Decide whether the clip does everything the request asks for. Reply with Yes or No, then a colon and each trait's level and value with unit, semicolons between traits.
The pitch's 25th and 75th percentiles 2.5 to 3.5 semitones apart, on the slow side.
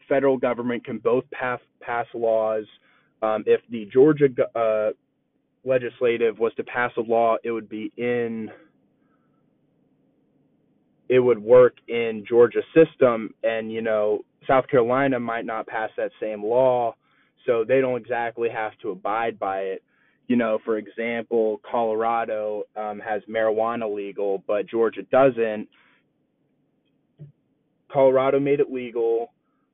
Yes: average, 3.1 semitones; slow, 130 wpm